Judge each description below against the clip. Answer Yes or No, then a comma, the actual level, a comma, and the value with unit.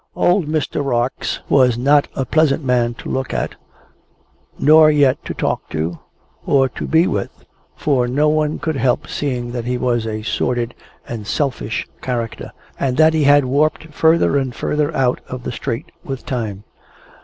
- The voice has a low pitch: Yes, low, 130 Hz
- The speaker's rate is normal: Yes, average, 165 wpm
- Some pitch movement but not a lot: Yes, average, 3.6 semitones